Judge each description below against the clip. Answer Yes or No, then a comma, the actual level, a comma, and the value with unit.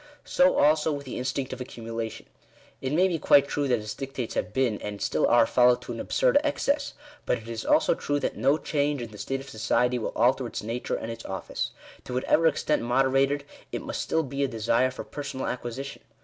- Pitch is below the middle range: Yes, low, 130 Hz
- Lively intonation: No, average, 3.6 semitones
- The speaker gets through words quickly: Yes, fast, 220 wpm